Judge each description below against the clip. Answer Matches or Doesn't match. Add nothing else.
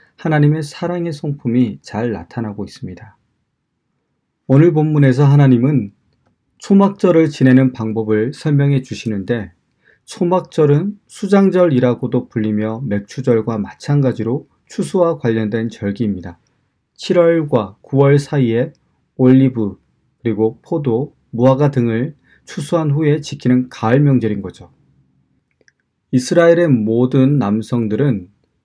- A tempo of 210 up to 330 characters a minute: Matches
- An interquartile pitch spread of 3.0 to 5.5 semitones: Matches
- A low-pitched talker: Matches